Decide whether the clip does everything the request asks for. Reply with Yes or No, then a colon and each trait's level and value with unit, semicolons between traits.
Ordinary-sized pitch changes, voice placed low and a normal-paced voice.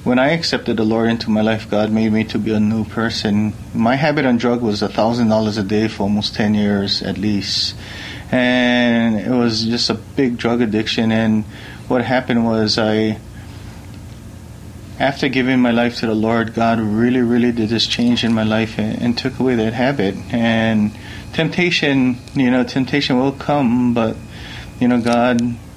No: narrow, 2.2 semitones; low, 115 Hz; average, 175 wpm